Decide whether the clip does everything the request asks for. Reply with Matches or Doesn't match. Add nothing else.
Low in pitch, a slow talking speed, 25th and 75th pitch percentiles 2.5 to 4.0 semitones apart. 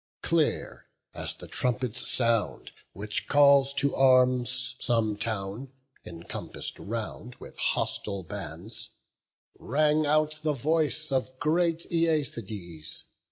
Doesn't match